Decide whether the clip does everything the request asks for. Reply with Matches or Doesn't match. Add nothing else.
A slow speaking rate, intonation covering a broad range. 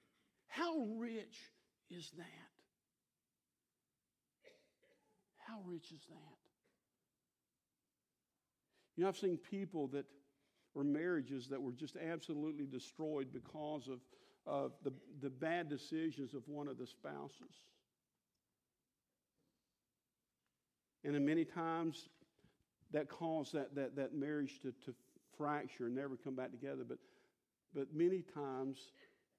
Doesn't match